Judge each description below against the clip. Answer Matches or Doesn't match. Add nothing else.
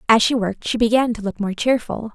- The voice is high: Matches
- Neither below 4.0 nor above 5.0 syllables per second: Doesn't match